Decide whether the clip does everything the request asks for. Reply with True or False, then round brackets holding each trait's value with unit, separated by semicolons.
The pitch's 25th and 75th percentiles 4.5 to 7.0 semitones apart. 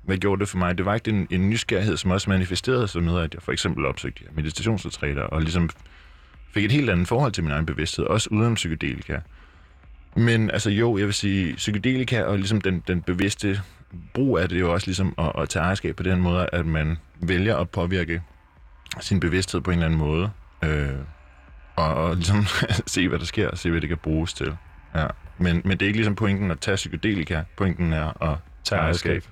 False (3.8 semitones)